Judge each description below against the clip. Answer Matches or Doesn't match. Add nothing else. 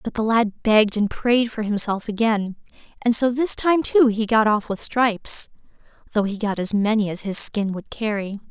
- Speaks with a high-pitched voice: Matches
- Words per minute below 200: Doesn't match